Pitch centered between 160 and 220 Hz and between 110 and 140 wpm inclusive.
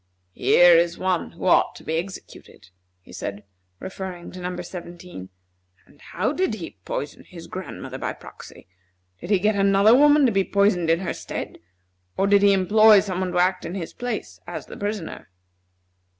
No: medium, 185 Hz; average, 180 wpm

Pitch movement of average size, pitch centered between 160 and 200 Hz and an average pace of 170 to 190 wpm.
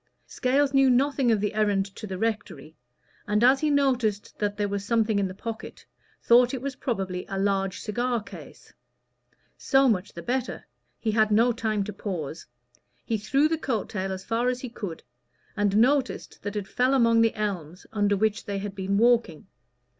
No: average, 3.7 semitones; high, 215 Hz; average, 185 wpm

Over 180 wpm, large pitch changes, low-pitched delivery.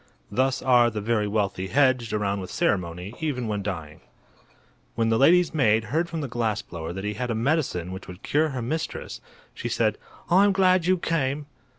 Yes: average, 190 wpm; wide, 6.8 semitones; low, 120 Hz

